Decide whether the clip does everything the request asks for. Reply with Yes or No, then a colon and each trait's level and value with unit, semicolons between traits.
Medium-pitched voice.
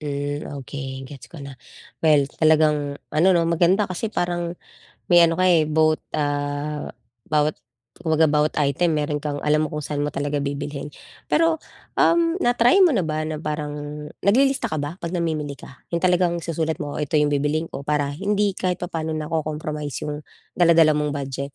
Yes: medium, 155 Hz